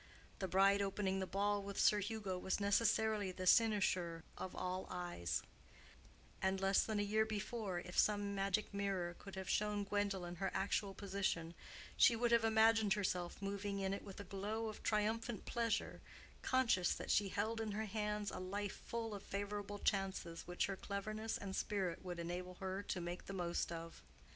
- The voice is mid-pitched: No, high, 200 Hz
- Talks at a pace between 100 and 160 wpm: No, average, 175 wpm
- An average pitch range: No, narrow, 2.0 semitones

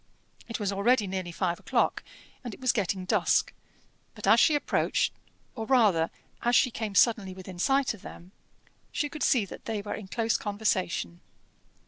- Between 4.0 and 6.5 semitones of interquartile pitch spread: Yes, average, 4.3 semitones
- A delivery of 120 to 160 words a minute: No, average, 170 wpm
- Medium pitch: No, high, 210 Hz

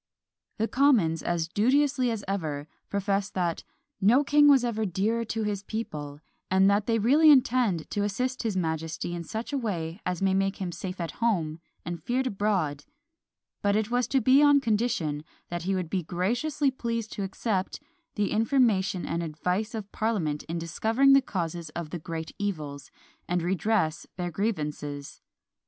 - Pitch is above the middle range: Yes, high, 195 Hz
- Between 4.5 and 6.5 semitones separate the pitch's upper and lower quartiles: Yes, wide, 5.4 semitones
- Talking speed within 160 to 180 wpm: Yes, average, 170 wpm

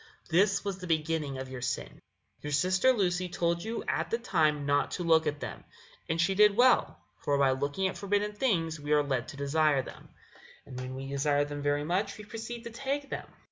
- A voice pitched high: No, medium, 165 Hz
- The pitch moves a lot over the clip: Yes, wide, 5.9 semitones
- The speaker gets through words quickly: Yes, fast, 215 wpm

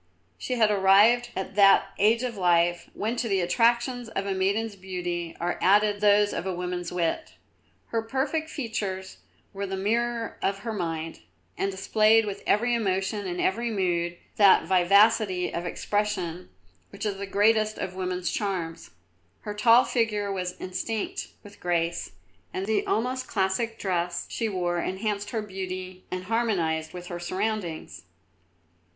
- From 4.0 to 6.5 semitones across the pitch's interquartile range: No, average, 3.4 semitones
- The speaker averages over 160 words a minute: No, average, 150 wpm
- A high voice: Yes, high, 195 Hz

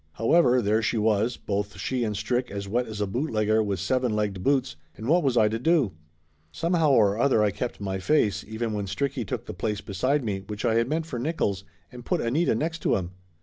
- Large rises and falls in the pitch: No, average, 4.2 semitones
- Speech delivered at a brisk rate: Yes, fast, 225 wpm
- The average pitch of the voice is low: Yes, low, 110 Hz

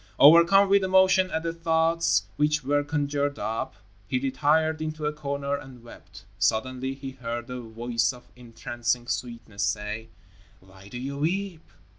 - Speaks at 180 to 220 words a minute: No, average, 150 wpm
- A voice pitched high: No, medium, 140 Hz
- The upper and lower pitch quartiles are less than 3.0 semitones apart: No, average, 4.9 semitones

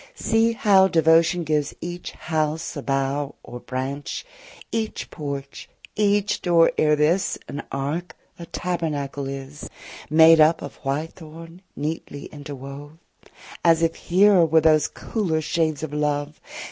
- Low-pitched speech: No, medium, 155 Hz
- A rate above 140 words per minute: No, slow, 135 wpm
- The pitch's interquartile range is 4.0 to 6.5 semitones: No, average, 2.9 semitones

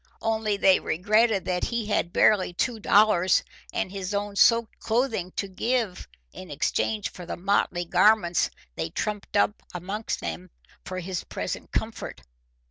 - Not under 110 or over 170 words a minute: Yes, average, 145 wpm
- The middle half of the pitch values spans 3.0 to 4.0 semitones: Yes, average, 3.3 semitones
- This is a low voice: No, high, 200 Hz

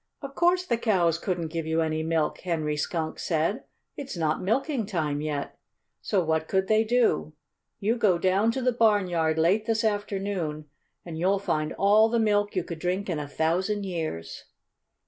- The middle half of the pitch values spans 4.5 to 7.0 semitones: Yes, average, 5.0 semitones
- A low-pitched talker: No, medium, 185 Hz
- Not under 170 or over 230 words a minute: Yes, average, 175 wpm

